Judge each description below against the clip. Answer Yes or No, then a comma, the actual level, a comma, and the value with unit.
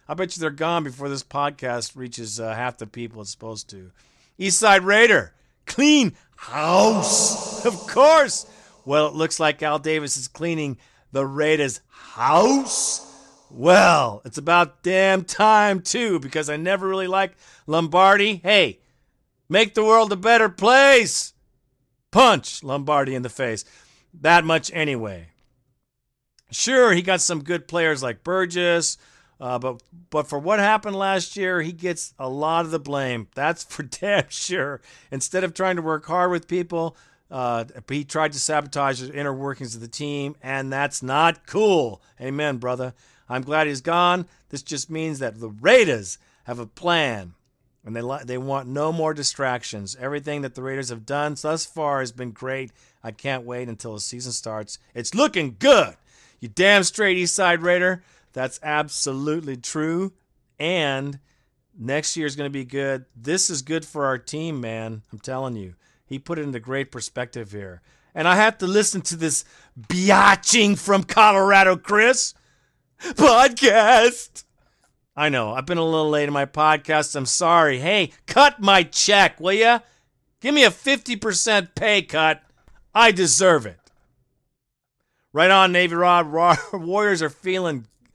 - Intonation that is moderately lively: No, wide, 5.9 semitones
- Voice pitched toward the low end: No, medium, 150 Hz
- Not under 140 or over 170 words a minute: Yes, average, 160 wpm